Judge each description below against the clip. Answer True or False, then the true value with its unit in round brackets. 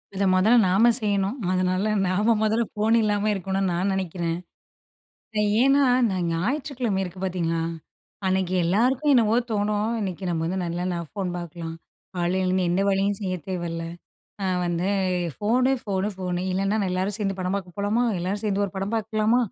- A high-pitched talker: True (195 Hz)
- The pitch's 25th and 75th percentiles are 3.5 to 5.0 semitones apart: False (2.7 semitones)